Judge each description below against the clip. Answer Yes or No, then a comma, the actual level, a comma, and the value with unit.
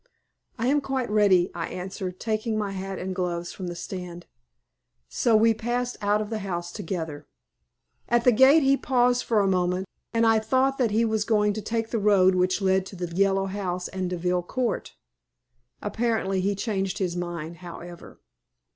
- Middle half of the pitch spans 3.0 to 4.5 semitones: Yes, average, 3.8 semitones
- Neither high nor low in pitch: No, high, 195 Hz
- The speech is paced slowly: No, average, 180 wpm